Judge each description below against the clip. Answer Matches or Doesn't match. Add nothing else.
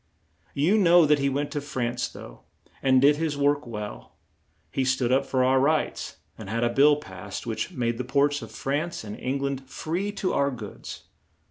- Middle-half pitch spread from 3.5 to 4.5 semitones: Doesn't match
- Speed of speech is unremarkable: Matches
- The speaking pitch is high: Doesn't match